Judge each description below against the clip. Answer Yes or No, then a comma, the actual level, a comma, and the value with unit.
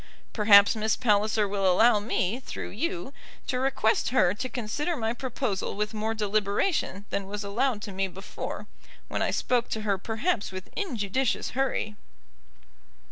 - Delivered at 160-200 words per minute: No, average, 150 wpm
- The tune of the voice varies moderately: Yes, average, 3.8 semitones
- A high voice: Yes, high, 215 Hz